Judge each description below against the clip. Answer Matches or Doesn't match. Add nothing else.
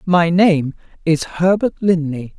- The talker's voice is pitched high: Doesn't match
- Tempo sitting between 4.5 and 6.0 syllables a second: Doesn't match